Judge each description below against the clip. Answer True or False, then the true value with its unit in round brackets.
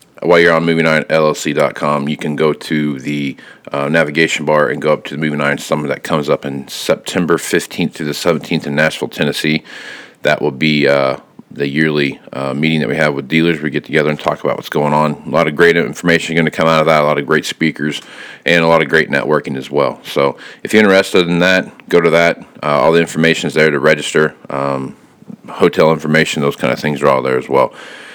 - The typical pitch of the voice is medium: False (75 Hz)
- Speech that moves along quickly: True (230 wpm)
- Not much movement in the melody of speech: True (1.9 semitones)